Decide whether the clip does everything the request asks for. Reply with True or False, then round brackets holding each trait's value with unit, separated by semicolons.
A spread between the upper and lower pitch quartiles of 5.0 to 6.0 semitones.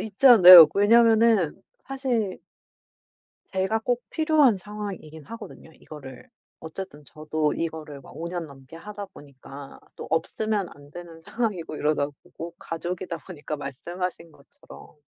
True (5.6 semitones)